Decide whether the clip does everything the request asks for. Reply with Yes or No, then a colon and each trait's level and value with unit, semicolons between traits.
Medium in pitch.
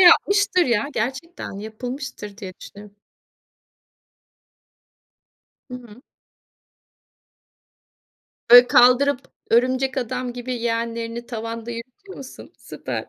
No: high, 245 Hz